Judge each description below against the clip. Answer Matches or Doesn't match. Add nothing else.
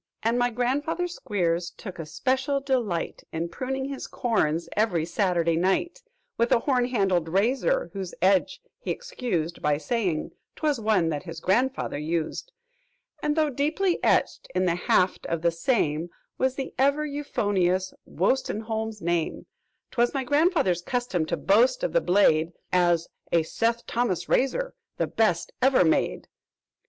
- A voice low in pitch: Doesn't match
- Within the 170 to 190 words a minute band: Doesn't match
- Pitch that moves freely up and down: Matches